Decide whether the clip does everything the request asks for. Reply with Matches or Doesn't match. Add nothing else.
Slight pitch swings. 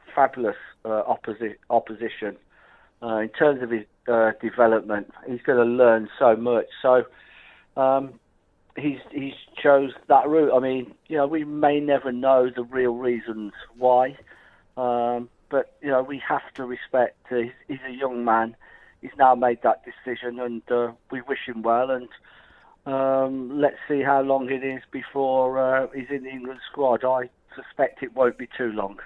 Matches